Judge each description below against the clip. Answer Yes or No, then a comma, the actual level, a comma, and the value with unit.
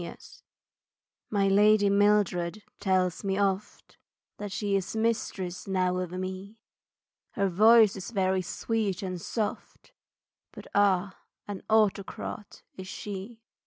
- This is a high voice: Yes, high, 195 Hz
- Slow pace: Yes, slow, 120 wpm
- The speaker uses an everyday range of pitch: No, narrow, 1.9 semitones